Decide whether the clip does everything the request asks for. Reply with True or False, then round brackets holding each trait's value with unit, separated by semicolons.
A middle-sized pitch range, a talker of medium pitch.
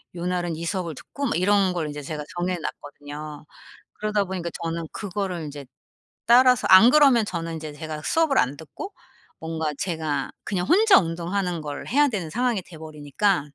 True (4.8 semitones; 175 Hz)